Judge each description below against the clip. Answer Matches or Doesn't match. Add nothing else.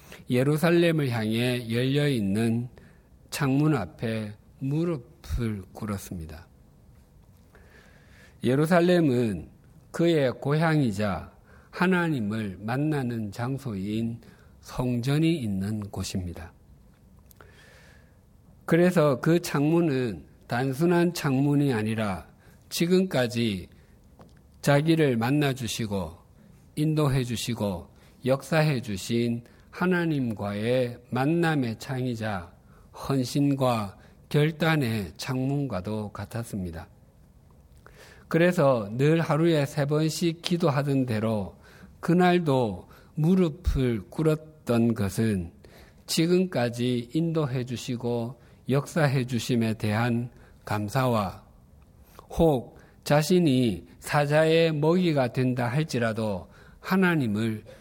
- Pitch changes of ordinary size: Doesn't match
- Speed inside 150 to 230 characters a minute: Matches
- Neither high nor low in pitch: Doesn't match